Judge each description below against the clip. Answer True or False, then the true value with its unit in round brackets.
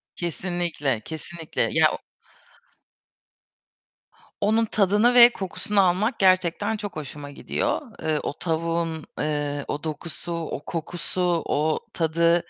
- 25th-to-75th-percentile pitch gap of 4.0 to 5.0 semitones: False (3.2 semitones)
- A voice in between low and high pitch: True (170 Hz)